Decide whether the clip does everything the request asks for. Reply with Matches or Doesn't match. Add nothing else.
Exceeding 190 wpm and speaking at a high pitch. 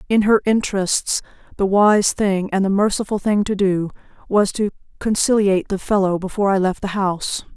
Doesn't match